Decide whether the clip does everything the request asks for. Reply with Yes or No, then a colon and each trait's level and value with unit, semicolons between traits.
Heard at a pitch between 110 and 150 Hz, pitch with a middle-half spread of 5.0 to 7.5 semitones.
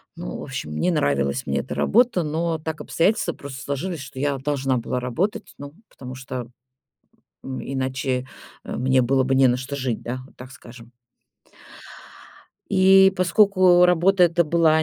Yes: medium, 140 Hz; average, 5.3 semitones